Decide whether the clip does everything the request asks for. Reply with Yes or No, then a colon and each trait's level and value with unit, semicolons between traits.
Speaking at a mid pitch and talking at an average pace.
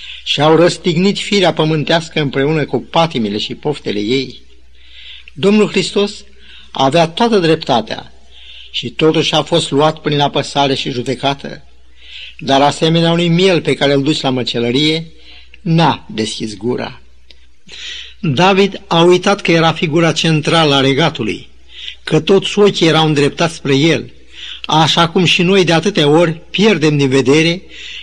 Yes: medium, 155 Hz; average, 135 wpm